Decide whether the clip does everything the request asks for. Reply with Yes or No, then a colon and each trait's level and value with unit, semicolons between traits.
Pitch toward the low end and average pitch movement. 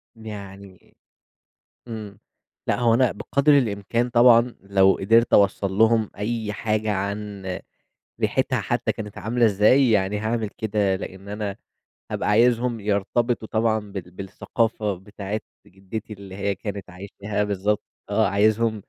No: low, 105 Hz; narrow, 2.2 semitones